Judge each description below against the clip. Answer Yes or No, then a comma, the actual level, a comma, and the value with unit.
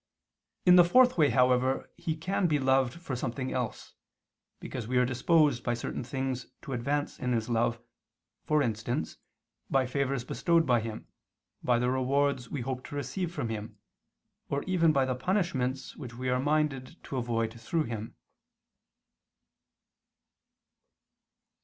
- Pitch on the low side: Yes, low, 130 Hz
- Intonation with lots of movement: No, average, 3.3 semitones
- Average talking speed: Yes, average, 145 wpm